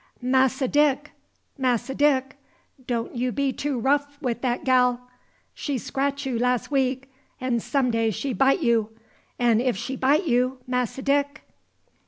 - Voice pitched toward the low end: No, very high, 260 Hz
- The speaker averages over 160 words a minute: No, average, 150 wpm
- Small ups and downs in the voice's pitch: Yes, narrow, 2.2 semitones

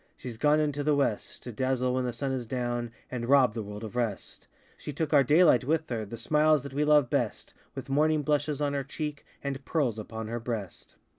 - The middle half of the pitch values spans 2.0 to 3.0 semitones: No, average, 3.8 semitones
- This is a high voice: No, low, 135 Hz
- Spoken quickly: Yes, fast, 220 wpm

